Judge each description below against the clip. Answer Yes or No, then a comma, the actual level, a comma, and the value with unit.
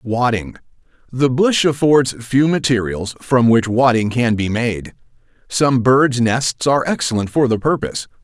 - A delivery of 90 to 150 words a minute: Yes, average, 140 wpm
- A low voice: Yes, low, 125 Hz